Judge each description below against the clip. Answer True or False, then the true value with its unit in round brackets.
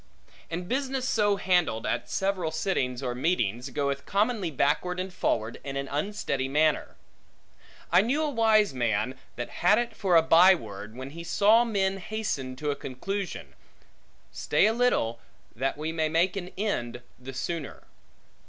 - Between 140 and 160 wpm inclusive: True (155 wpm)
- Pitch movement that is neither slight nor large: False (7.1 semitones)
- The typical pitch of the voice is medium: True (165 Hz)